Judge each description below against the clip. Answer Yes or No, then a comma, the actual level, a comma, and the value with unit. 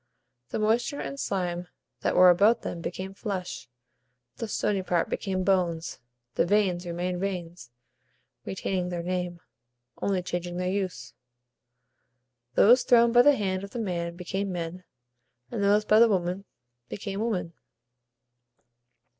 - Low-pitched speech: No, medium, 185 Hz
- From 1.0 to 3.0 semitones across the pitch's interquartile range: Yes, narrow, 2.6 semitones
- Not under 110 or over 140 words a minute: Yes, slow, 135 wpm